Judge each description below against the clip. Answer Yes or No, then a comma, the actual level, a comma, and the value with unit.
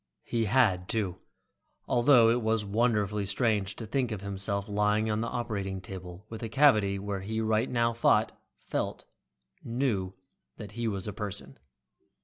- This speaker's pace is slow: No, average, 155 wpm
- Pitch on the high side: No, low, 105 Hz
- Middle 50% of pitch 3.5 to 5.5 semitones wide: No, average, 2.7 semitones